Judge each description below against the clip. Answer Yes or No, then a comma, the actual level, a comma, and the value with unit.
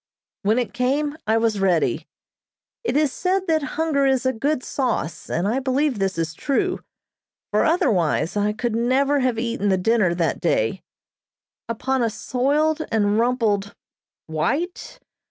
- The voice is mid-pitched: No, high, 245 Hz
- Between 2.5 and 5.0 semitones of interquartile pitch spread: No, wide, 5.6 semitones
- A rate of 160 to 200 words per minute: No, average, 150 wpm